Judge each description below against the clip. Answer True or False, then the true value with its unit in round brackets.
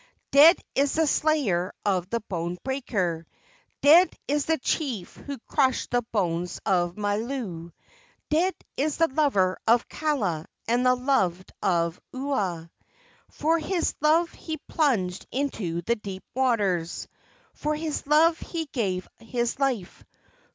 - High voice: True (245 Hz)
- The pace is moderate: False (130 wpm)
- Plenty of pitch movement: True (8.2 semitones)